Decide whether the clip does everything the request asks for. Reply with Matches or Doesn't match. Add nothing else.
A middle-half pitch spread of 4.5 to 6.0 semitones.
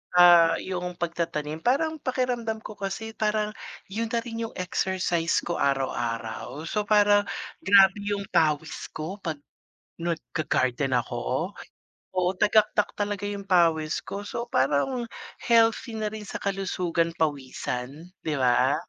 Matches